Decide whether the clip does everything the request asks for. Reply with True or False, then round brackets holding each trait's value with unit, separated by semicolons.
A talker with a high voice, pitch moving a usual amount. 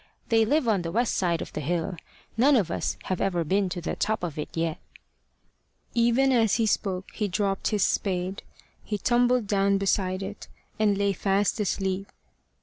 True (200 Hz; 3.2 semitones)